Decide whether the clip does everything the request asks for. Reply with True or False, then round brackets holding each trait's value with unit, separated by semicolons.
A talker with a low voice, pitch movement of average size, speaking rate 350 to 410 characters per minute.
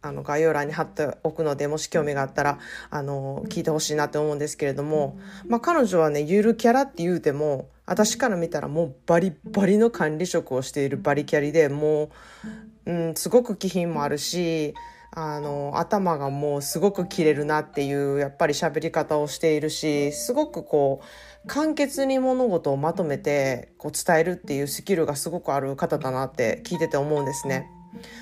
False (160 Hz; 4.5 semitones; 375 characters per minute)